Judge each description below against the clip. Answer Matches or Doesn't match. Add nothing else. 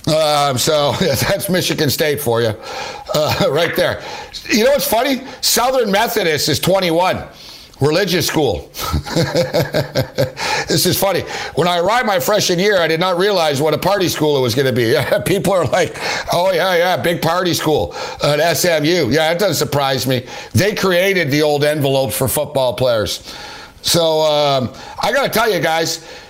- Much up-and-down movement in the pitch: Doesn't match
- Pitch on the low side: Doesn't match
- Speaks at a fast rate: Doesn't match